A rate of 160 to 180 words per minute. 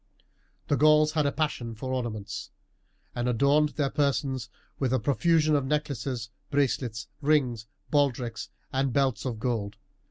No: slow, 135 wpm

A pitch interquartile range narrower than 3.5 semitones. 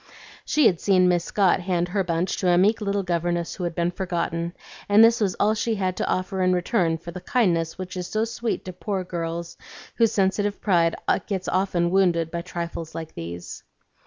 Yes: narrow, 2.6 semitones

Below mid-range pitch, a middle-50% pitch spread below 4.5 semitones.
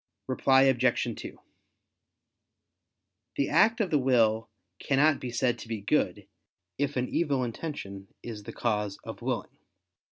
Yes: low, 125 Hz; average, 4.1 semitones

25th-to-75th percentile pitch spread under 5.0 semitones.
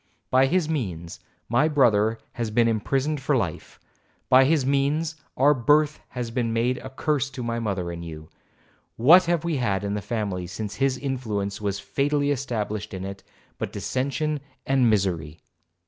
No: average, 5.3 semitones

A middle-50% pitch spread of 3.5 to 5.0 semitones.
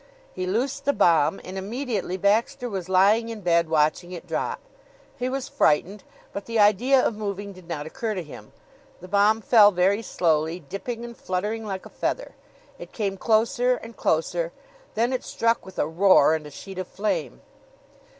Yes: average, 4.2 semitones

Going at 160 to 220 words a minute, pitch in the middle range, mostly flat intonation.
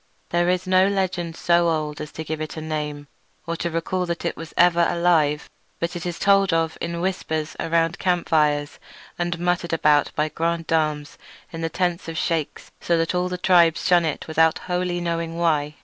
Yes: average, 190 wpm; medium, 170 Hz; narrow, 1.8 semitones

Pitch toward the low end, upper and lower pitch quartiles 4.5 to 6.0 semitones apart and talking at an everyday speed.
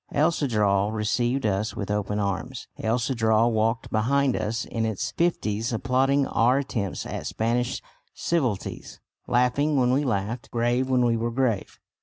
No: low, 120 Hz; average, 3.2 semitones; average, 150 wpm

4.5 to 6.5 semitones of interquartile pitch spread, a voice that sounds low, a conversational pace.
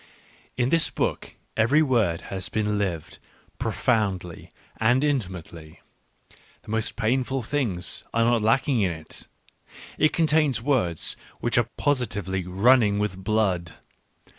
No: wide, 5.5 semitones; low, 110 Hz; slow, 125 wpm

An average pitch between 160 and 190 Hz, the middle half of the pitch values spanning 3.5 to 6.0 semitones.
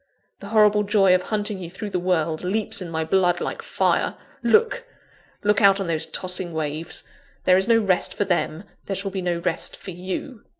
No: medium, 185 Hz; average, 2.9 semitones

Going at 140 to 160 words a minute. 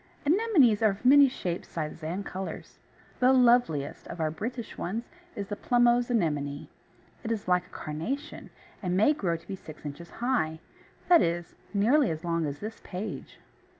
No: average, 170 wpm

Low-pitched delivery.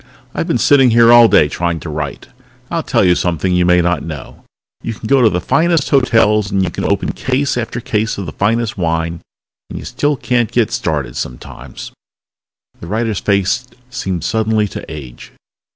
Yes: low, 105 Hz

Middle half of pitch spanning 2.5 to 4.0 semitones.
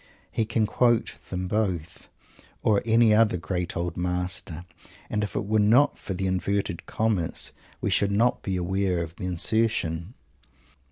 Yes: average, 3.6 semitones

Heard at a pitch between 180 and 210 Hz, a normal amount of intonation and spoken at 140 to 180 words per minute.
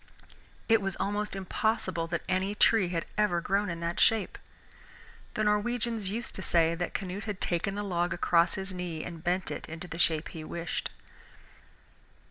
Yes: medium, 185 Hz; average, 3.3 semitones; average, 170 wpm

